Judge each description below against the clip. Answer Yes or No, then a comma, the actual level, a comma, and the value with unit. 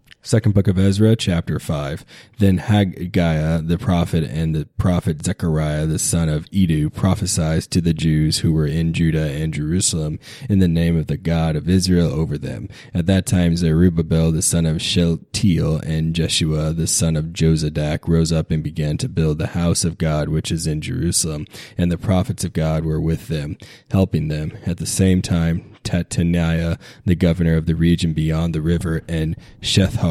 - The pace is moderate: Yes, average, 180 wpm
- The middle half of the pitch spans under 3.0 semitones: Yes, narrow, 2.5 semitones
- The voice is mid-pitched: No, very low, 85 Hz